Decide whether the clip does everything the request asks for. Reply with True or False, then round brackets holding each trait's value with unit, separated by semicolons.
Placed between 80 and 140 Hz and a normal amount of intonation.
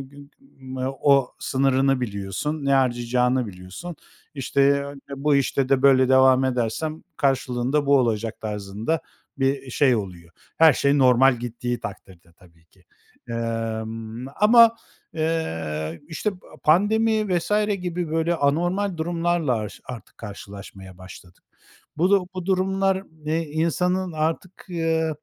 False (135 Hz; 6.0 semitones)